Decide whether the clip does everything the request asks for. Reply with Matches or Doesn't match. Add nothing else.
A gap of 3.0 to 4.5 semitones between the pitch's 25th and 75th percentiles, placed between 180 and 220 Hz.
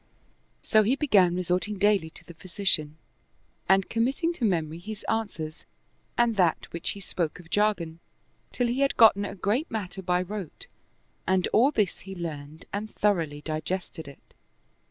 Matches